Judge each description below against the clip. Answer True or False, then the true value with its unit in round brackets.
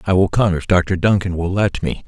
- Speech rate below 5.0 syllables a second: False (5.2 syllables/s)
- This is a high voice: False (95 Hz)